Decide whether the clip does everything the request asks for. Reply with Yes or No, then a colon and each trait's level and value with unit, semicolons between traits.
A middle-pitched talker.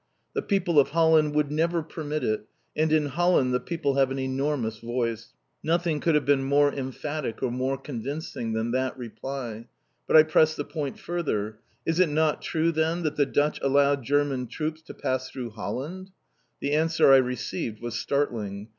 Yes: medium, 145 Hz